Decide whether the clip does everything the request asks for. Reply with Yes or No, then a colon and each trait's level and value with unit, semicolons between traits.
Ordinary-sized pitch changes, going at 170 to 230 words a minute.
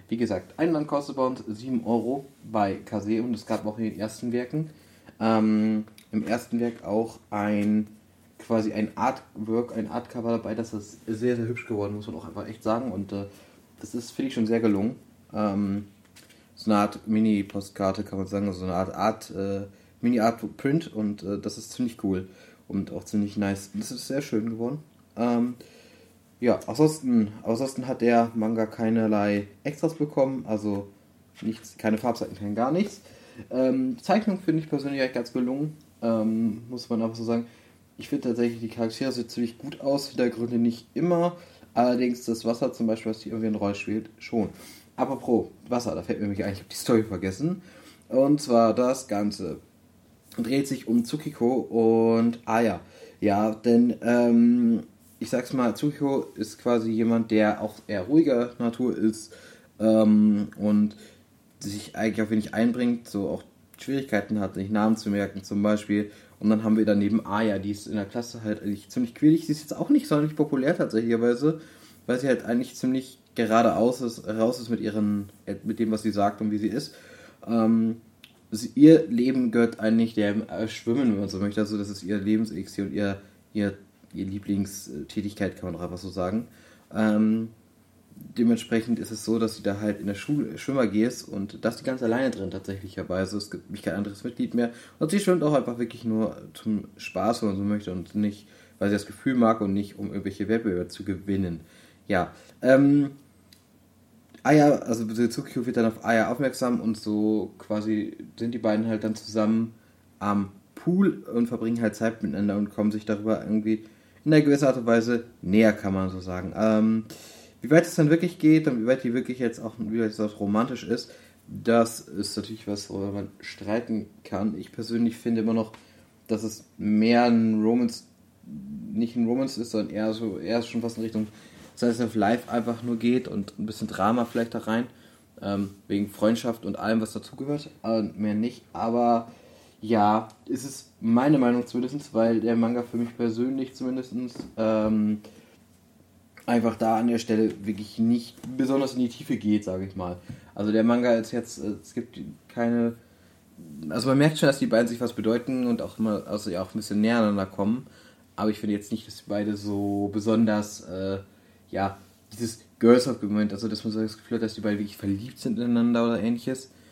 No: narrow, 2.3 semitones; fast, 190 wpm